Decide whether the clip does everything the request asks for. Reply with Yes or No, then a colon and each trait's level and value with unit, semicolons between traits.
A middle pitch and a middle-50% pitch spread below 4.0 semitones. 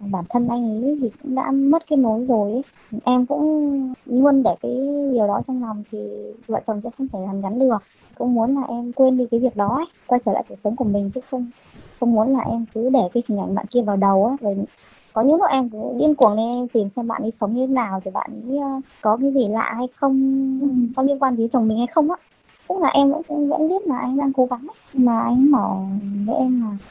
No: high, 245 Hz; average, 3.6 semitones